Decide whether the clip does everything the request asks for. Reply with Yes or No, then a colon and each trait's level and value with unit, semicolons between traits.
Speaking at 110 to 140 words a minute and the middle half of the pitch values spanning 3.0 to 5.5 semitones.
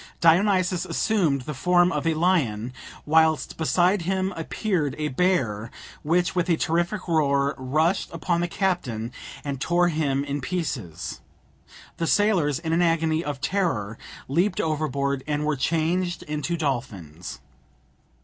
Yes: slow, 135 wpm; average, 4.2 semitones